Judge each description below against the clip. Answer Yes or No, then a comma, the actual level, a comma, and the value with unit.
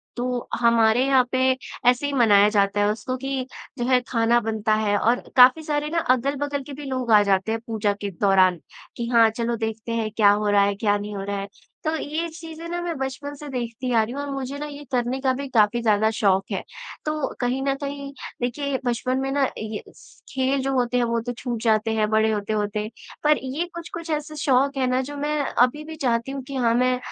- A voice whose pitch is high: Yes, high, 245 Hz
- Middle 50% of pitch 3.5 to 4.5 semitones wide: Yes, average, 4.1 semitones